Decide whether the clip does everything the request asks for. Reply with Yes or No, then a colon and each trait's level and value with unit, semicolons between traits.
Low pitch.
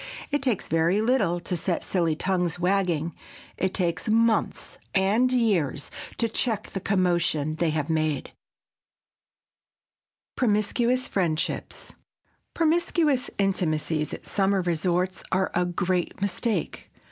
No: medium, 185 Hz